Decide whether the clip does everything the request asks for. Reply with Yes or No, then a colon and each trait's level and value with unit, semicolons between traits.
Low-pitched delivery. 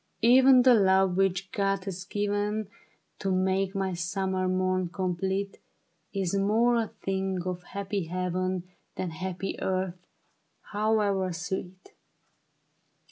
No: high, 190 Hz